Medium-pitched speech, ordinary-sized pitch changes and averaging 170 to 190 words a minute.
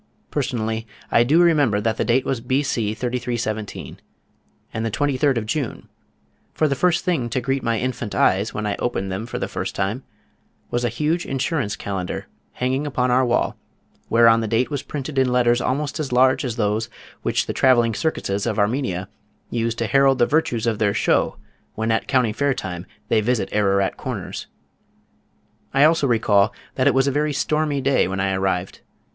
No: low, 120 Hz; average, 3.9 semitones; average, 185 wpm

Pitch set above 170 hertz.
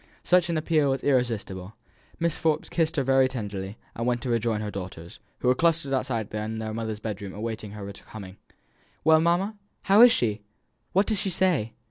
No: low, 120 Hz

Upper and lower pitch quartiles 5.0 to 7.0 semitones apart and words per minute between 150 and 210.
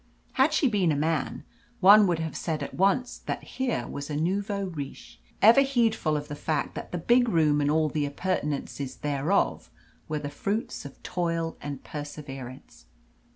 Yes: average, 5.3 semitones; average, 170 wpm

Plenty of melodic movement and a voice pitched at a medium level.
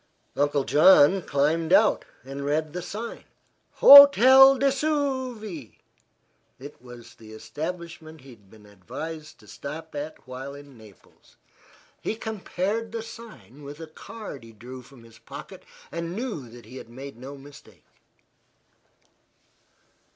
Yes: wide, 8.1 semitones; medium, 150 Hz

